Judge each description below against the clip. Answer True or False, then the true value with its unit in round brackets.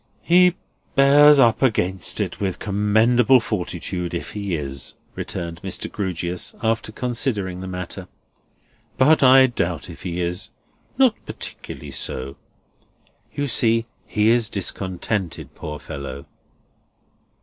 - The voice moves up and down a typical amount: False (5.8 semitones)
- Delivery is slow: True (115 wpm)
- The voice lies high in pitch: False (100 Hz)